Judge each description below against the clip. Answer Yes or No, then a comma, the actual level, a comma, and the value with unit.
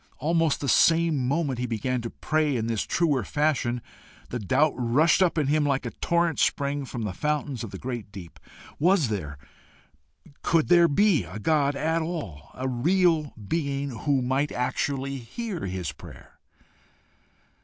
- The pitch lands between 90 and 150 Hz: Yes, medium, 140 Hz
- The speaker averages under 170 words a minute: Yes, average, 160 wpm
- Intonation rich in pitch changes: No, average, 4.9 semitones